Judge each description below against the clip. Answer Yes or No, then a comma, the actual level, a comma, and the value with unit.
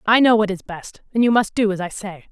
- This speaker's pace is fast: Yes, fast, 310 wpm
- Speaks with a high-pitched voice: Yes, high, 210 Hz